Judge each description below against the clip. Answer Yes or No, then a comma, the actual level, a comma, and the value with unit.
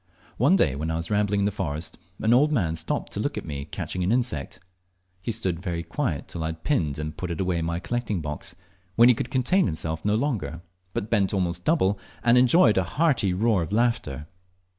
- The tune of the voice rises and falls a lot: Yes, wide, 6.4 semitones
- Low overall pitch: Yes, very low, 95 Hz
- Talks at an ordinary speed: No, fast, 220 wpm